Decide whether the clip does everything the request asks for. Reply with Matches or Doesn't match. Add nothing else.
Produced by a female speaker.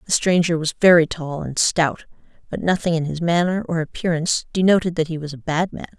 Matches